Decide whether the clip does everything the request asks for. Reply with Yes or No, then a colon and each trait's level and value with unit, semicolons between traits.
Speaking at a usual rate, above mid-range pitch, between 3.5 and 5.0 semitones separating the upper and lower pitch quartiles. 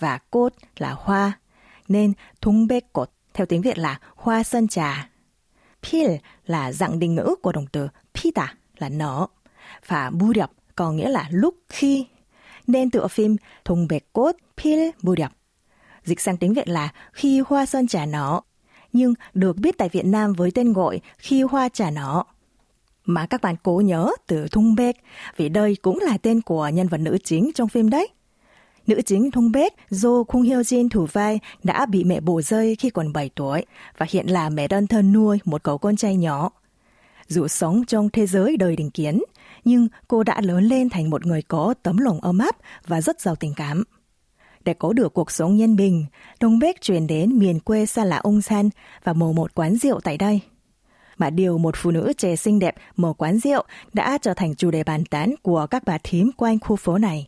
No: average, 205 wpm; high, 195 Hz; wide, 5.4 semitones